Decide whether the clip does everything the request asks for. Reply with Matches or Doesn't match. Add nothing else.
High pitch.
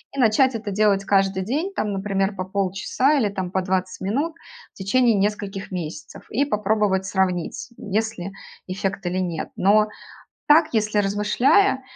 Matches